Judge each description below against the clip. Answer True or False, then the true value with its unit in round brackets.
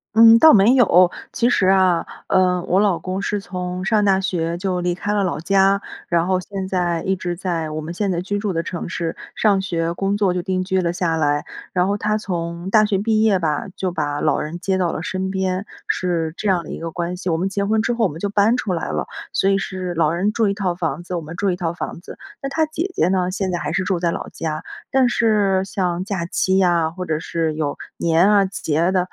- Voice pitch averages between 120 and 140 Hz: False (185 Hz)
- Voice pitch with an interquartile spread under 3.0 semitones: True (2.6 semitones)